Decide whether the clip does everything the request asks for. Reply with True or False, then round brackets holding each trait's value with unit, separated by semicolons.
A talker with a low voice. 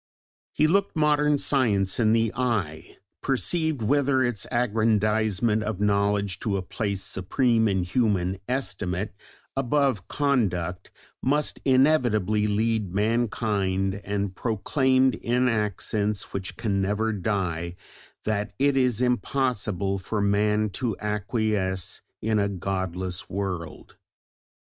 True (105 Hz)